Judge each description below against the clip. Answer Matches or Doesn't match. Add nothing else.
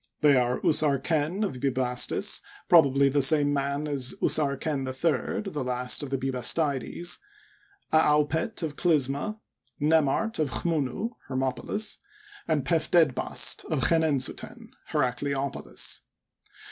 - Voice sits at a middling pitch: Matches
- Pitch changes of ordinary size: Matches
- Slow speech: Matches